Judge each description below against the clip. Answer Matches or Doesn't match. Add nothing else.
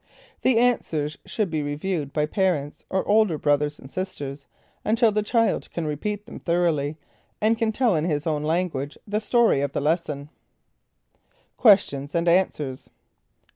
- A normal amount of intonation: Doesn't match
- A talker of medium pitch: Matches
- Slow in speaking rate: Doesn't match